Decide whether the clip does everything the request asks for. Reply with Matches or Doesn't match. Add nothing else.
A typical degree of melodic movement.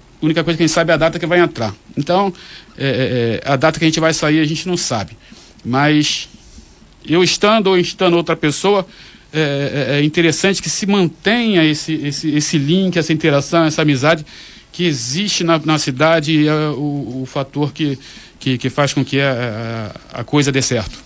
Matches